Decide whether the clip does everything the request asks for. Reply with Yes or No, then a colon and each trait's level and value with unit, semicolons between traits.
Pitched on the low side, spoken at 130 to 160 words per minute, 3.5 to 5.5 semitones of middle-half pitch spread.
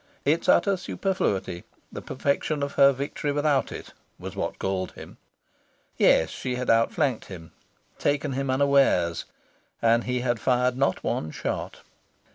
Yes: low, 130 Hz; average, 140 wpm; average, 3.8 semitones